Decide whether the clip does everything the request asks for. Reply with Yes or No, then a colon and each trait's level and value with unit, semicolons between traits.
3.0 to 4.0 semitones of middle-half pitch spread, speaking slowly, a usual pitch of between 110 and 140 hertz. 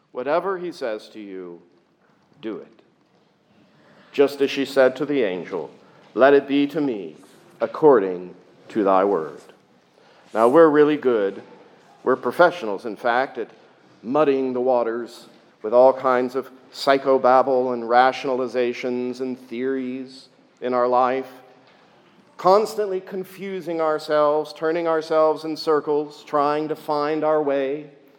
Yes: average, 3.3 semitones; slow, 125 wpm; low, 135 Hz